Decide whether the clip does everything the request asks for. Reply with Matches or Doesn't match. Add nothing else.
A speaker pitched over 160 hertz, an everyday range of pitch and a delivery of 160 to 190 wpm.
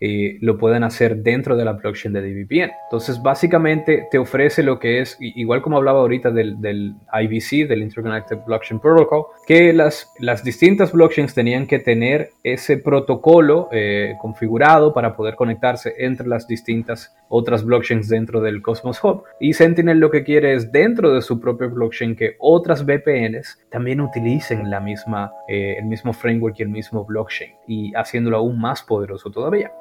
Doesn't match